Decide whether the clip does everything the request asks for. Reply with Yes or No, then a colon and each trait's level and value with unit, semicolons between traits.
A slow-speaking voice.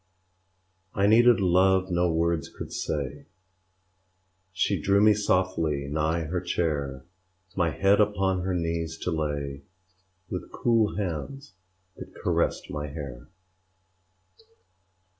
Yes: slow, 110 wpm